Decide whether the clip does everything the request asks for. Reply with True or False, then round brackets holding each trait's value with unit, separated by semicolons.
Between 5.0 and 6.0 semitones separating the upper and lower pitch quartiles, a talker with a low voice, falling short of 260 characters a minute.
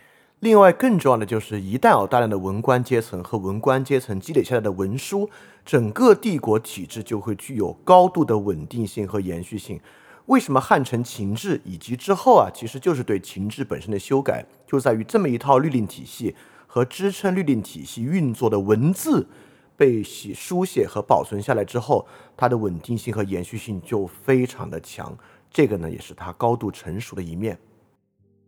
False (5.3 semitones; 115 Hz; 285 characters per minute)